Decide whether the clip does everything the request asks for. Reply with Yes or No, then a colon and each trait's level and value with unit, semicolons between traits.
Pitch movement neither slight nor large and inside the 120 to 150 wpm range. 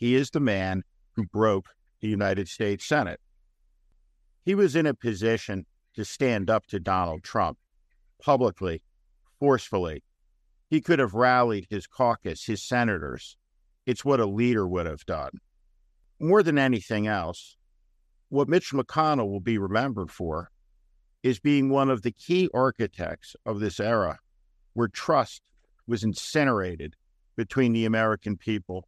No: wide, 8.1 semitones; average, 140 wpm